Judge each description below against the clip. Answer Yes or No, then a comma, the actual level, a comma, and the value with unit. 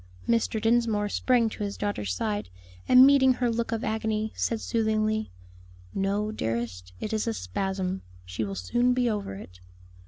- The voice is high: Yes, high, 215 Hz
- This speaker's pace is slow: No, average, 160 wpm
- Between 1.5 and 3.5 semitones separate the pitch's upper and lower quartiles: No, average, 4.0 semitones